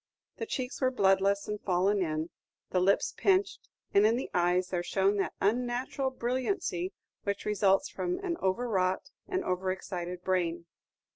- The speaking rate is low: No, average, 155 wpm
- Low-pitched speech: No, high, 200 Hz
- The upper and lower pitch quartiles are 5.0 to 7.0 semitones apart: Yes, wide, 5.4 semitones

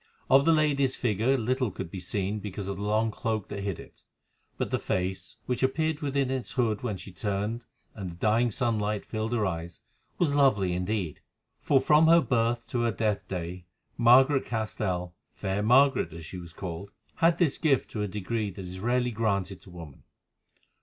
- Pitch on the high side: No, low, 110 Hz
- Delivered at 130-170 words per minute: No, average, 180 wpm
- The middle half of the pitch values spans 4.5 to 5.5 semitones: Yes, average, 5.0 semitones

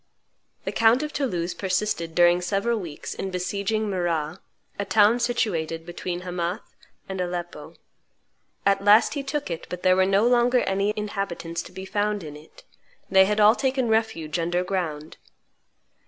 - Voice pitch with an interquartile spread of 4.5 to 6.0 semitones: No, average, 3.7 semitones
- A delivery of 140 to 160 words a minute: Yes, average, 155 wpm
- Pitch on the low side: No, high, 190 Hz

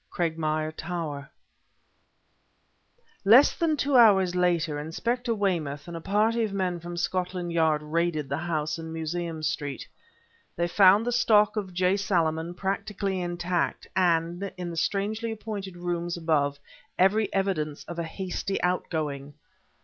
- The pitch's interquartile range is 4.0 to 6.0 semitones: No, average, 3.4 semitones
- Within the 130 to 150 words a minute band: Yes, slow, 135 wpm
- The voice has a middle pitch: Yes, medium, 175 Hz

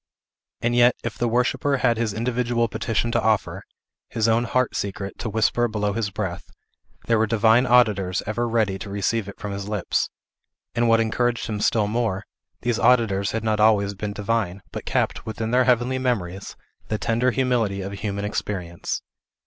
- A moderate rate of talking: Yes, average, 180 wpm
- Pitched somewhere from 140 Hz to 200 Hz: No, low, 110 Hz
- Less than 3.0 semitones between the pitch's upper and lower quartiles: Yes, narrow, 2.6 semitones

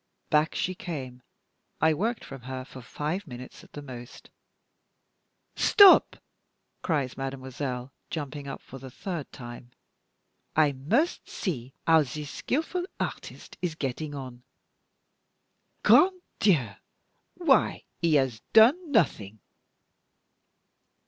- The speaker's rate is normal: No, slow, 110 wpm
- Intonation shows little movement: No, average, 5.2 semitones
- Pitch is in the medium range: Yes, medium, 145 Hz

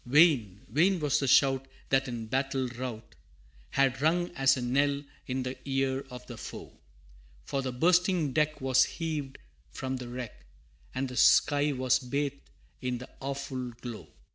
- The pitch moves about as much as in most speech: No, narrow, 2.2 semitones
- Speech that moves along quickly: No, average, 160 wpm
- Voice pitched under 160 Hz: Yes, low, 135 Hz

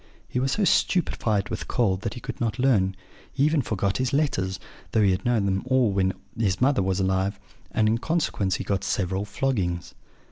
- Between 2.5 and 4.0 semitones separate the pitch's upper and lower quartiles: No, average, 5.1 semitones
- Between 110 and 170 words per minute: No, average, 200 wpm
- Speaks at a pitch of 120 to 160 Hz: No, low, 105 Hz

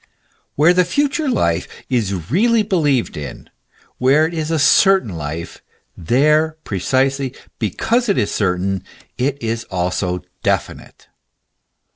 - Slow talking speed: Yes, slow, 125 wpm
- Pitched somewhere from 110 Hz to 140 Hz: Yes, low, 135 Hz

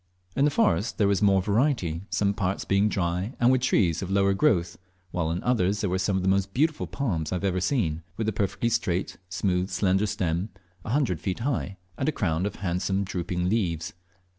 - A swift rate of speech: Yes, fast, 215 wpm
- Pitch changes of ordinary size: Yes, average, 3.4 semitones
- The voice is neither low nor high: No, very low, 95 Hz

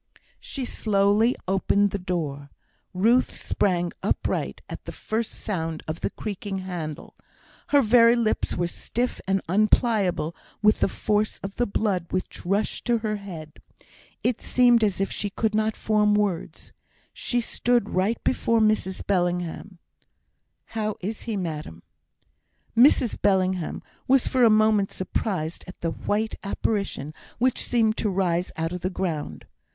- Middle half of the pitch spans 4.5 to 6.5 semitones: No, average, 3.5 semitones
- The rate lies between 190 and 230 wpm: No, average, 145 wpm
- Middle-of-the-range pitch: No, high, 200 Hz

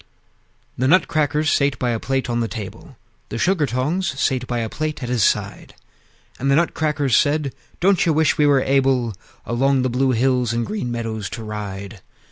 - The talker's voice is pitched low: Yes, low, 130 Hz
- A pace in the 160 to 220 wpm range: Yes, average, 185 wpm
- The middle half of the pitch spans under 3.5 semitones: No, average, 4.0 semitones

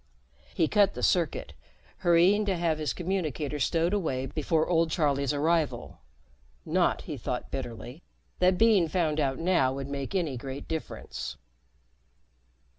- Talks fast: No, slow, 135 wpm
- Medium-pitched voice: Yes, medium, 160 Hz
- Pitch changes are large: No, average, 4.2 semitones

